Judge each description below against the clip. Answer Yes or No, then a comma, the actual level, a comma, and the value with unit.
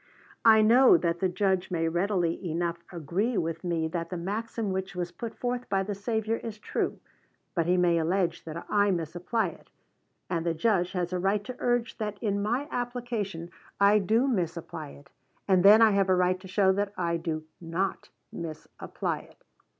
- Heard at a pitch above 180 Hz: Yes, high, 190 Hz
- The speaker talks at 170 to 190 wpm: Yes, average, 185 wpm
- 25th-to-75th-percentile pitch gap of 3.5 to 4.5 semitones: Yes, average, 3.8 semitones